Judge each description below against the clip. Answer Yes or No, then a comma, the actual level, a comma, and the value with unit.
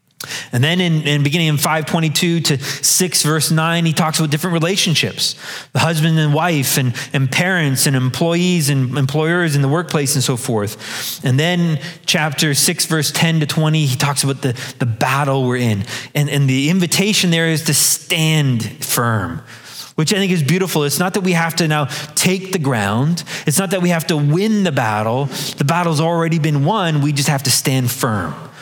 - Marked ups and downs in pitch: No, average, 3.5 semitones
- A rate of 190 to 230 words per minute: Yes, average, 195 wpm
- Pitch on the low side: No, medium, 155 Hz